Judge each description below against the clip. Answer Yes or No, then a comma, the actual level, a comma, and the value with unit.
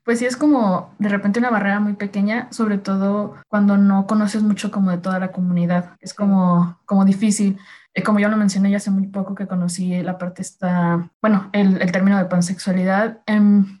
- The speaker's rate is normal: No, fast, 195 wpm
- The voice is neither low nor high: No, high, 195 Hz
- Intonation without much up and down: Yes, narrow, 1.9 semitones